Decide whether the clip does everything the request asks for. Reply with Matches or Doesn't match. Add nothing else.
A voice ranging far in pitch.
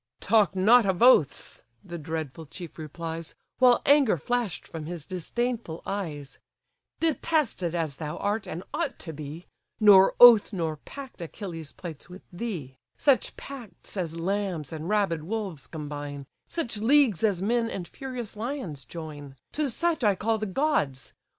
Matches